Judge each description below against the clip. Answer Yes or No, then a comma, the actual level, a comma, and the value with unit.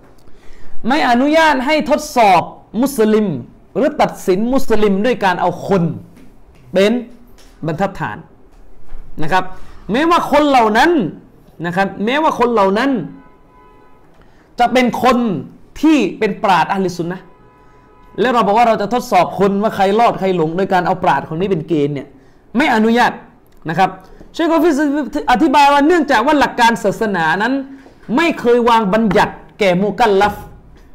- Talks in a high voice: Yes, high, 215 Hz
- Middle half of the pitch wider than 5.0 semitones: Yes, wide, 5.4 semitones